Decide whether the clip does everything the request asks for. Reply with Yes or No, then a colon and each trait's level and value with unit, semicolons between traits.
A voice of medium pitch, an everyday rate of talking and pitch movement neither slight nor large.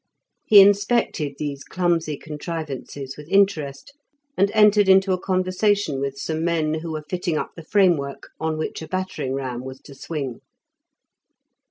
Yes: medium, 160 Hz; average, 150 wpm; average, 5.0 semitones